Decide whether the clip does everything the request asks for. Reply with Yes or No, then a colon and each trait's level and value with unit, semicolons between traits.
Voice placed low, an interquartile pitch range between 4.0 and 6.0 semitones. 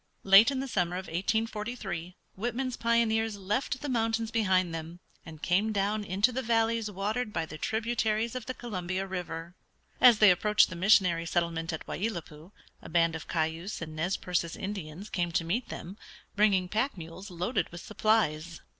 No: high, 195 Hz; average, 4.6 semitones